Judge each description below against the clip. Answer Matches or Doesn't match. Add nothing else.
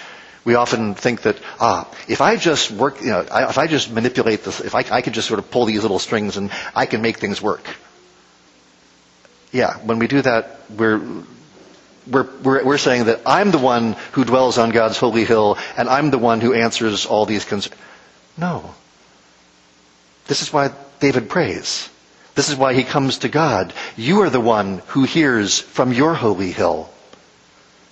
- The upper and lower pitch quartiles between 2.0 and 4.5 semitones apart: Doesn't match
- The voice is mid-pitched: Doesn't match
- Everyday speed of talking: Matches